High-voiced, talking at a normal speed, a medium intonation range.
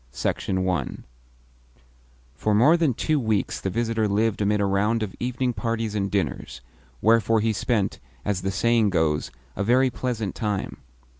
No: low, 110 Hz; average, 155 wpm; average, 3.0 semitones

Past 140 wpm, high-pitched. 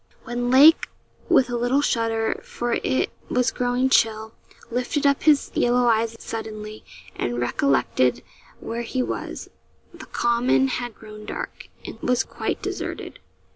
No: slow, 135 wpm; high, 240 Hz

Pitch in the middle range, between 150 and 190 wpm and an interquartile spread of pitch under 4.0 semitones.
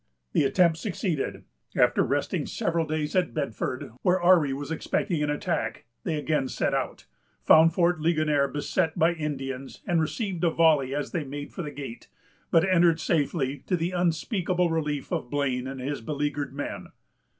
Yes: medium, 155 Hz; average, 165 wpm; average, 3.1 semitones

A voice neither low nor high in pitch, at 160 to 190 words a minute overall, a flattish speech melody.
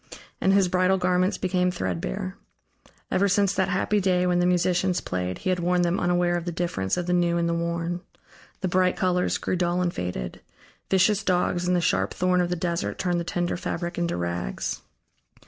No: medium, 180 Hz; average, 200 wpm; narrow, 1.1 semitones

